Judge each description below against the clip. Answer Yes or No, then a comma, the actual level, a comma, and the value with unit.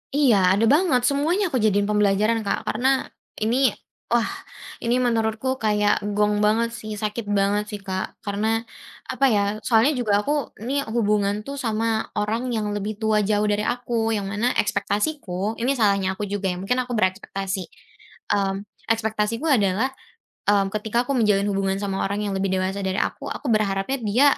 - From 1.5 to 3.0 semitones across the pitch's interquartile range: Yes, narrow, 2.5 semitones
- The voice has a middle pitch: No, high, 210 Hz